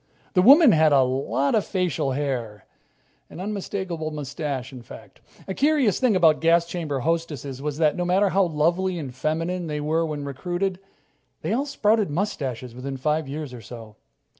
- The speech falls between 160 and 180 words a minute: Yes, average, 170 wpm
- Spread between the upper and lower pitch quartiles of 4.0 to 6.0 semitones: Yes, average, 5.0 semitones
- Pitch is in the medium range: Yes, medium, 155 Hz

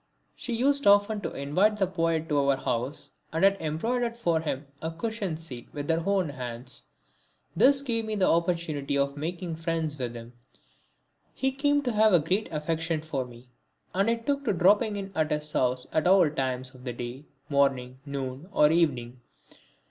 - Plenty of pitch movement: Yes, wide, 6.3 semitones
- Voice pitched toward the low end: No, medium, 160 Hz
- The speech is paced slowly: No, average, 180 wpm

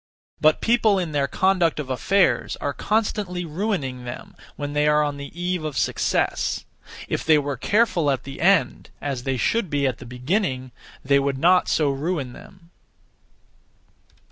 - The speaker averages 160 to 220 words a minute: Yes, average, 165 wpm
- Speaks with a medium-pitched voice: Yes, medium, 150 Hz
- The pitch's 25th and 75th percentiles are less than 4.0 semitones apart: No, average, 5.0 semitones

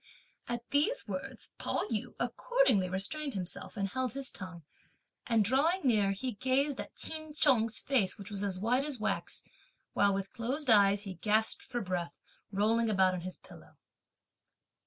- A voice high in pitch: Yes, high, 220 Hz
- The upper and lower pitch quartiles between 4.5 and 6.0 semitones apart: Yes, average, 5.1 semitones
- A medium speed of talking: Yes, average, 160 wpm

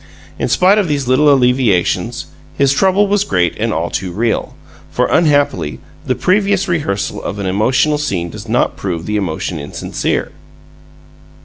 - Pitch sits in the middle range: No, low, 125 Hz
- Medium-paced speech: Yes, average, 150 wpm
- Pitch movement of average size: No, wide, 8.2 semitones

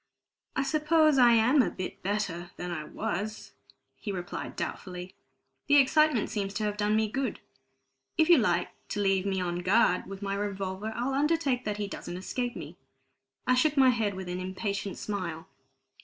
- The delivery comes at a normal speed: Yes, average, 175 wpm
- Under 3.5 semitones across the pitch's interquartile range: No, average, 5.2 semitones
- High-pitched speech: Yes, high, 210 Hz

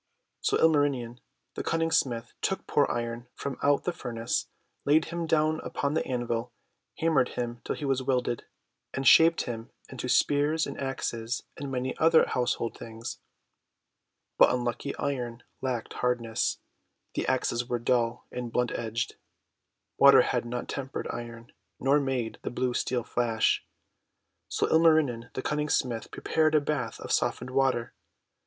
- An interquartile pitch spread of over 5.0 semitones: No, average, 3.4 semitones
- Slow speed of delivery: No, average, 150 wpm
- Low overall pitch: Yes, low, 125 Hz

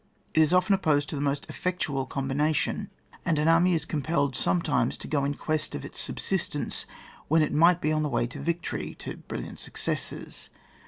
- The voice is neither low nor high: Yes, medium, 155 Hz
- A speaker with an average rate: Yes, average, 190 wpm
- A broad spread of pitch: No, average, 2.7 semitones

